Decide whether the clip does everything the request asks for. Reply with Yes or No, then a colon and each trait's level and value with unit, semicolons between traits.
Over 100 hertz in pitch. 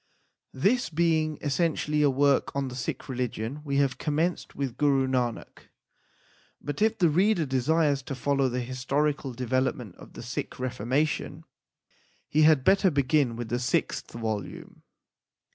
Yes: medium, 140 Hz